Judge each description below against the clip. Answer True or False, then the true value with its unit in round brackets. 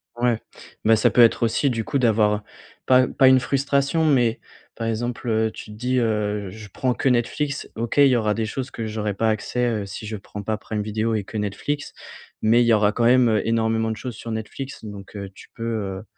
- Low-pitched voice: True (115 Hz)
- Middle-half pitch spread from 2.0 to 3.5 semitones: True (2.6 semitones)